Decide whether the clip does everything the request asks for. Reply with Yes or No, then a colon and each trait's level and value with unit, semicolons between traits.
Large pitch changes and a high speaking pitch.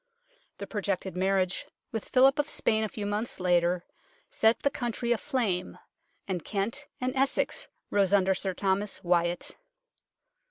No: average, 3.9 semitones; high, 200 Hz